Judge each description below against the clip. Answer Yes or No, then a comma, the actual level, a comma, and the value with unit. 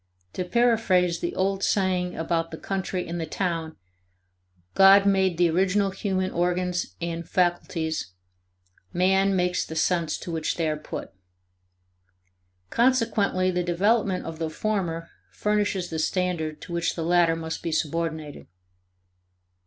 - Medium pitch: Yes, medium, 180 Hz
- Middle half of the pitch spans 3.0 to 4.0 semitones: No, narrow, 2.6 semitones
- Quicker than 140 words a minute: No, slow, 135 wpm